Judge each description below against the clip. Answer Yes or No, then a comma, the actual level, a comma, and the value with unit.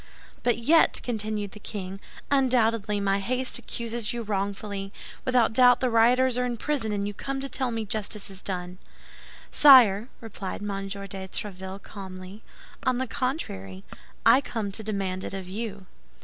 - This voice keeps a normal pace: Yes, average, 160 wpm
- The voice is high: Yes, high, 215 Hz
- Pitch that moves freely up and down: No, average, 3.8 semitones